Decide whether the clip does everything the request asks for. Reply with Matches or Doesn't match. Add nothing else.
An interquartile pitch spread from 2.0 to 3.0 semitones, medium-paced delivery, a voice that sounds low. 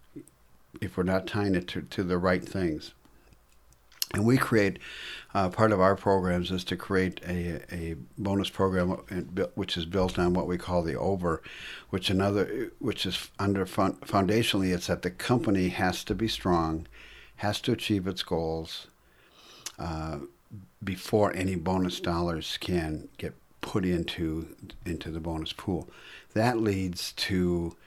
Matches